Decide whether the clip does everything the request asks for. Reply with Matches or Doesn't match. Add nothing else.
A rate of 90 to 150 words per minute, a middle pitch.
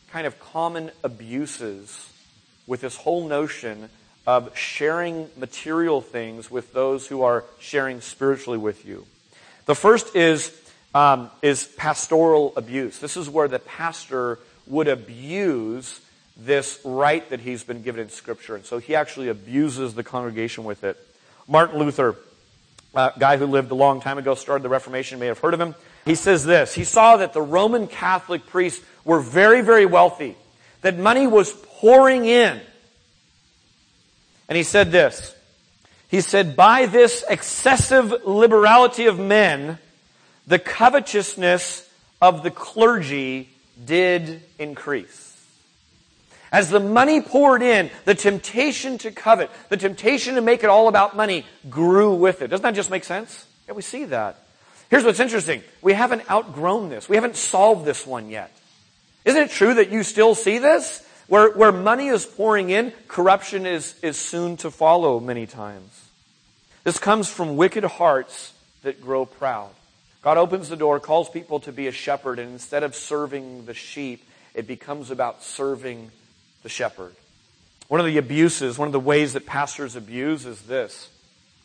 Doesn't match